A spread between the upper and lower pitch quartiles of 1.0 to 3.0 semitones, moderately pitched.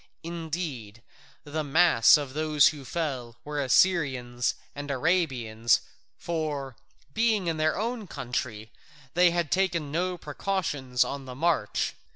No: average, 5.1 semitones; medium, 150 Hz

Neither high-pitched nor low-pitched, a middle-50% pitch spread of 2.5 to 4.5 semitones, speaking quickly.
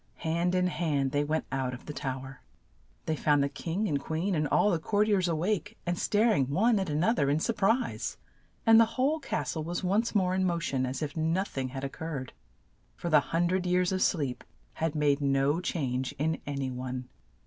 No: medium, 160 Hz; average, 5.0 semitones; fast, 230 wpm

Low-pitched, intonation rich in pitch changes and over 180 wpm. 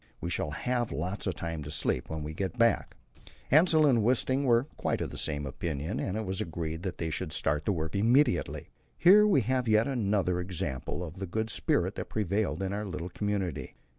Yes: very low, 95 Hz; wide, 6.1 semitones; fast, 205 wpm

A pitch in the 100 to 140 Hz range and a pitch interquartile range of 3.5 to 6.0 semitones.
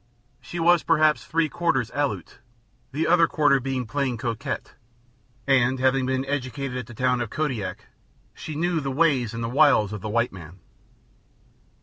Yes: low, 135 Hz; average, 4.0 semitones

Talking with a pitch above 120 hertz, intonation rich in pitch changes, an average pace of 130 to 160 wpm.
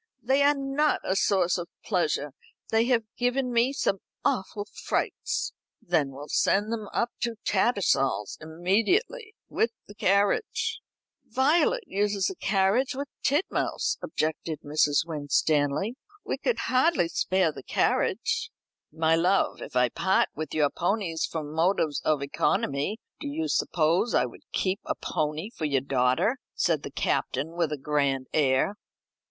Yes: high, 190 Hz; wide, 8.1 semitones; average, 145 wpm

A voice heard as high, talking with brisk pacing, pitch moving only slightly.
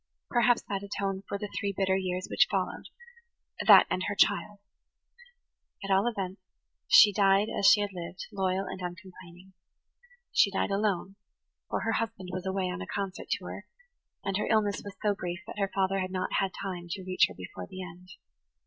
No: high, 195 Hz; average, 175 wpm; narrow, 1.6 semitones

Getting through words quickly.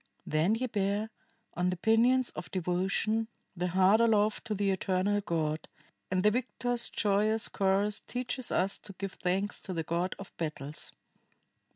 No: average, 155 wpm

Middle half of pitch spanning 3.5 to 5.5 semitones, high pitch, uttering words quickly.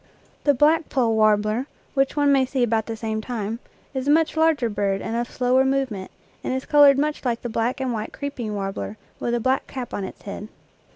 Yes: average, 3.9 semitones; high, 245 Hz; fast, 215 wpm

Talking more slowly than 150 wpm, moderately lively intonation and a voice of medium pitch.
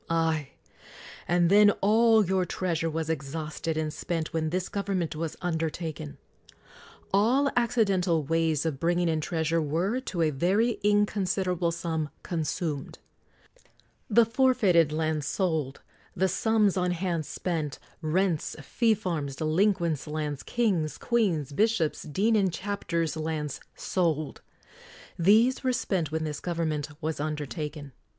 Yes: average, 140 wpm; average, 4.1 semitones; medium, 165 Hz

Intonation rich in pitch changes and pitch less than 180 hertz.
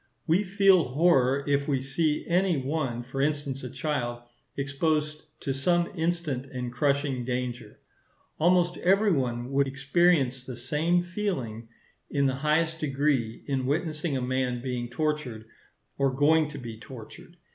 No: average, 4.0 semitones; medium, 140 Hz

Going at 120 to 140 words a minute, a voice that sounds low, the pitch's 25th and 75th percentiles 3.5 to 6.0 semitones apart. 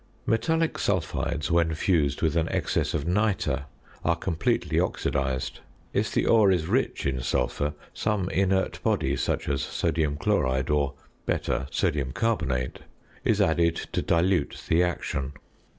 Yes: slow, 135 wpm; very low, 80 Hz; average, 4.9 semitones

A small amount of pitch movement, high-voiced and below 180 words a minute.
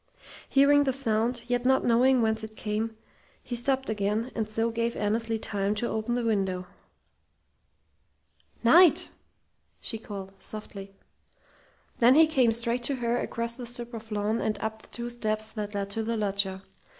Yes: narrow, 2.2 semitones; high, 225 Hz; average, 160 wpm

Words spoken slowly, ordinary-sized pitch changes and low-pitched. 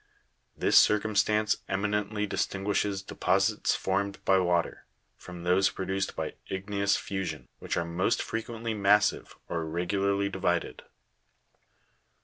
No: slow, 110 wpm; narrow, 1.8 semitones; low, 100 Hz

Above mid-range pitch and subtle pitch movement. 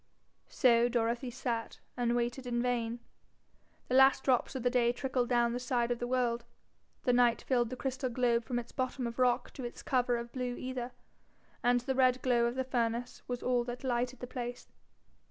Yes: high, 245 Hz; narrow, 1.1 semitones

